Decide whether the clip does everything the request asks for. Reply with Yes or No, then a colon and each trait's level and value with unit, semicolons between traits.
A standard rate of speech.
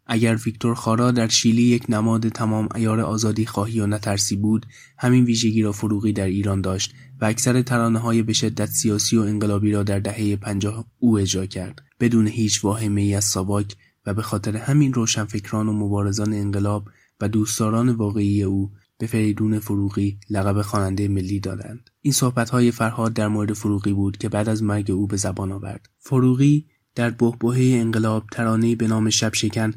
No: fast, 175 wpm